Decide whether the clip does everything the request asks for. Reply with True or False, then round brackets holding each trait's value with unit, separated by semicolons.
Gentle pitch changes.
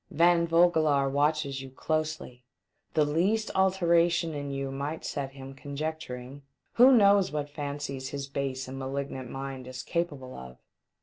False (3.6 semitones)